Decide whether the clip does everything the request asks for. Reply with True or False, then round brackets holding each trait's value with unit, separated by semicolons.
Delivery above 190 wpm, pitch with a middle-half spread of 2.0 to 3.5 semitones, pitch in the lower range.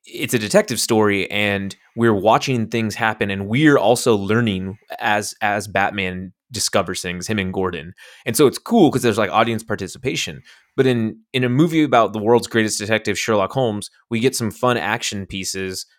False (180 wpm; 3.2 semitones; 110 Hz)